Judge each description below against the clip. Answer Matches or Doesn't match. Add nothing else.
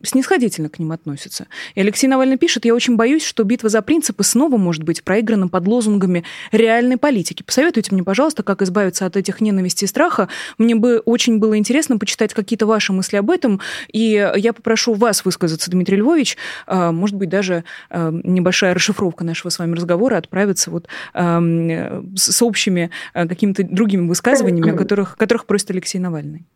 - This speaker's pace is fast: Matches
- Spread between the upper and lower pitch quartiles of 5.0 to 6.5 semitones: Doesn't match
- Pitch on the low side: Doesn't match